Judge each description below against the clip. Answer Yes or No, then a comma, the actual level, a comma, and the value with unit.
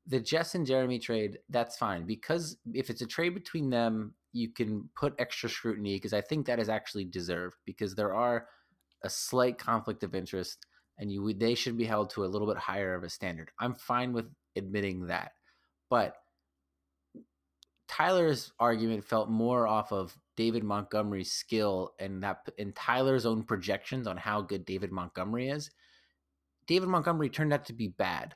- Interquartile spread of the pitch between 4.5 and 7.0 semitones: No, average, 4.1 semitones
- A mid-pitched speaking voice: No, low, 110 Hz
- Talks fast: No, average, 175 wpm